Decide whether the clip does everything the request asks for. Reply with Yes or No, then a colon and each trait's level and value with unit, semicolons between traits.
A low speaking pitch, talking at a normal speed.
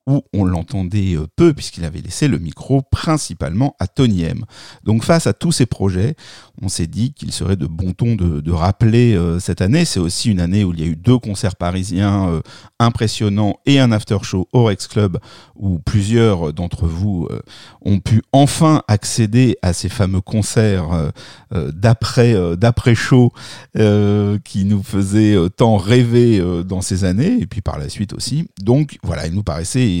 Yes: low, 105 Hz; average, 185 wpm